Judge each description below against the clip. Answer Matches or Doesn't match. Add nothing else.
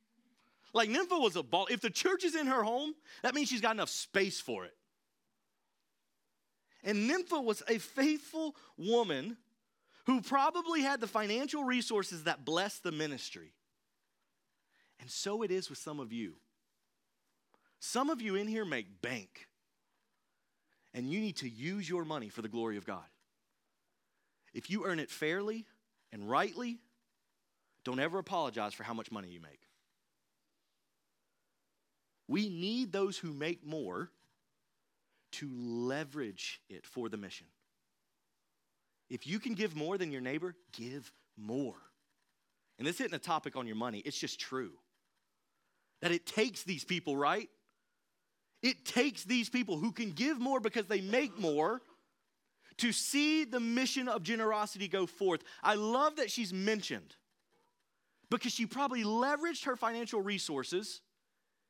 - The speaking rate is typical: Matches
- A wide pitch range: Matches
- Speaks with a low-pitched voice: Doesn't match